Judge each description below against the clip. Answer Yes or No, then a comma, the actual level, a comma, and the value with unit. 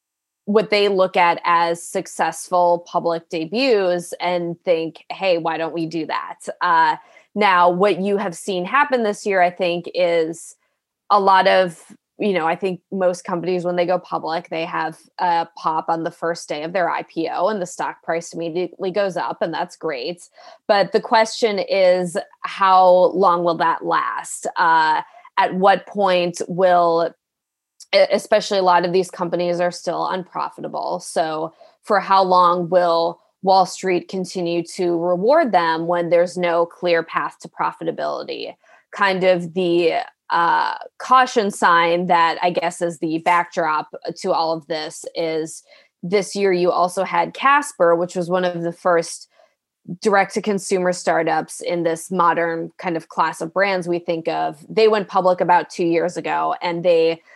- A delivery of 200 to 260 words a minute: No, average, 165 wpm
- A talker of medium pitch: Yes, medium, 180 Hz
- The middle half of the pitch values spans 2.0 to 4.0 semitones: Yes, average, 2.7 semitones